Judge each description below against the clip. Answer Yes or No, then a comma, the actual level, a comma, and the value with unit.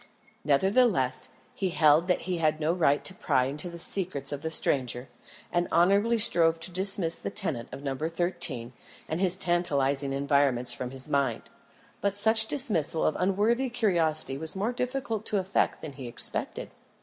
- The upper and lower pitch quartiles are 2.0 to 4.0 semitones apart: No, wide, 5.6 semitones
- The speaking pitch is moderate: Yes, medium, 165 Hz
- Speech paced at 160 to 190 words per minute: Yes, average, 165 wpm